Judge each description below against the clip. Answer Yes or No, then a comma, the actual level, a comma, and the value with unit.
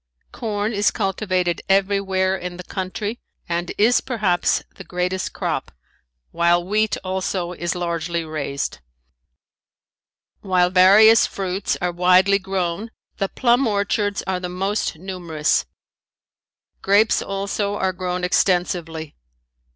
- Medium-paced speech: No, slow, 110 wpm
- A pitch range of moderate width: No, narrow, 2.3 semitones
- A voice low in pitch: No, medium, 185 Hz